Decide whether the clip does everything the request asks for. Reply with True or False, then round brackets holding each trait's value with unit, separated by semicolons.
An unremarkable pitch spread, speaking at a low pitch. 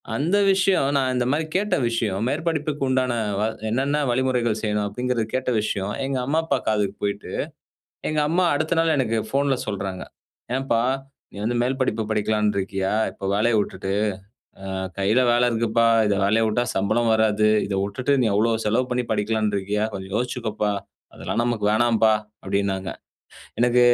True (3.8 semitones; 115 Hz)